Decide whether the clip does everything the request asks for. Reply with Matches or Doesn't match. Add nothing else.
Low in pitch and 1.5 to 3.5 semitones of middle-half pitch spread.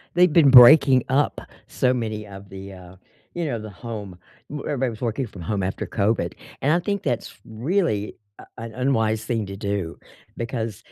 Doesn't match